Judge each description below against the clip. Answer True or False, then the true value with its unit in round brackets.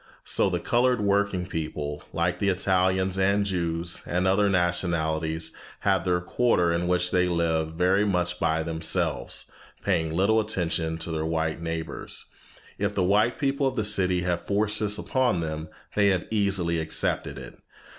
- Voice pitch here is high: False (90 Hz)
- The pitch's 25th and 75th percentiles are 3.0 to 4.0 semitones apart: True (3.3 semitones)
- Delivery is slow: False (160 wpm)